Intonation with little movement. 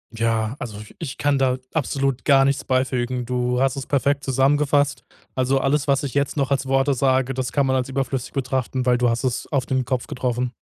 Yes: narrow, 1.8 semitones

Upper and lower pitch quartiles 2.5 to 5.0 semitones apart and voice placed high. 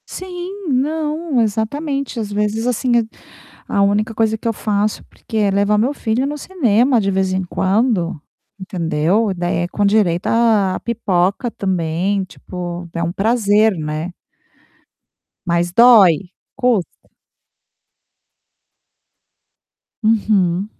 Yes: average, 4.1 semitones; high, 210 Hz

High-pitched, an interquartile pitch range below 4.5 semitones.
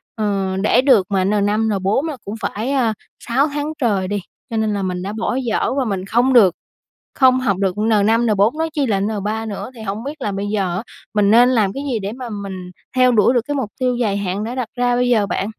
Yes: high, 220 Hz; average, 3.7 semitones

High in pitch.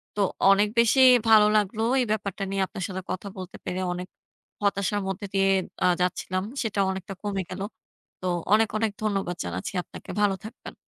Yes: high, 195 Hz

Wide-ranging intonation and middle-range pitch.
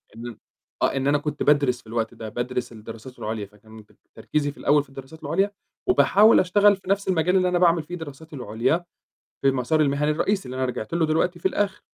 Yes: wide, 6.0 semitones; medium, 145 Hz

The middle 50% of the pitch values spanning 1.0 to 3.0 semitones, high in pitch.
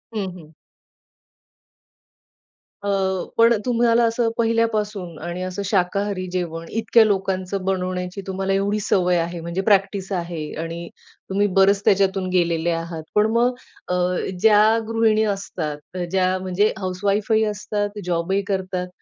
Yes: narrow, 2.5 semitones; high, 195 Hz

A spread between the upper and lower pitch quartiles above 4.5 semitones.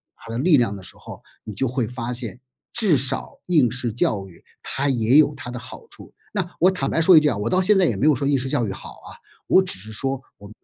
Yes: average, 5.0 semitones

